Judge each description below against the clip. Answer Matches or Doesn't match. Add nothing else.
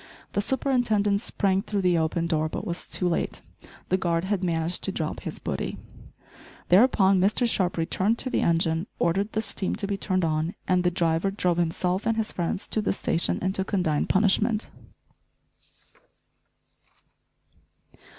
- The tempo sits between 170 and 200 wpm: Doesn't match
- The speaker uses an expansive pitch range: Doesn't match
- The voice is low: Doesn't match